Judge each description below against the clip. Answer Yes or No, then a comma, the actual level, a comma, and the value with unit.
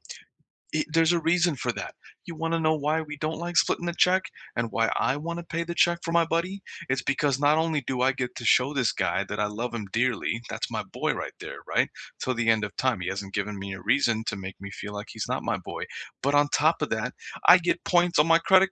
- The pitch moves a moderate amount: No, wide, 6.8 semitones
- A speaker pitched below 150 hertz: Yes, medium, 140 Hz